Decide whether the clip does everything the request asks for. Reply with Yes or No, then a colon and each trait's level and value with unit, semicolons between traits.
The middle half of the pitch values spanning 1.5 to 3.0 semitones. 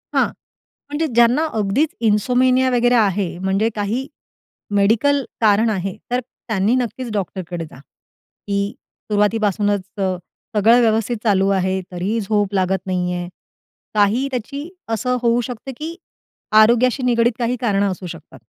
No: average, 3.9 semitones